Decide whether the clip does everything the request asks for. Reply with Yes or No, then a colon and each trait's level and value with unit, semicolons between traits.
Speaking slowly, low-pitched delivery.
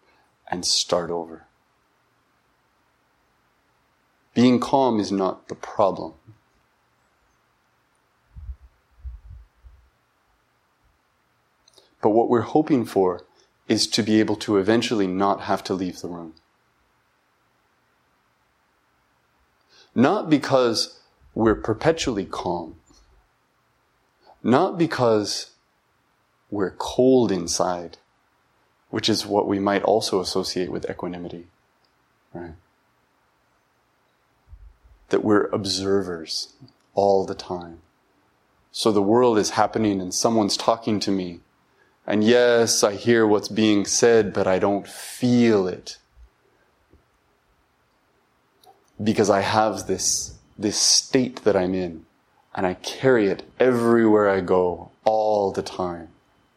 Yes: slow, 100 wpm; low, 100 Hz